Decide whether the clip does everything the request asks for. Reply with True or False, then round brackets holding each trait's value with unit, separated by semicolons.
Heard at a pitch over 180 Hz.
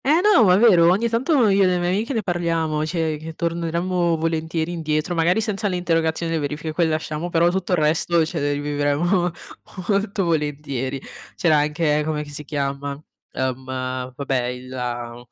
False (165 Hz)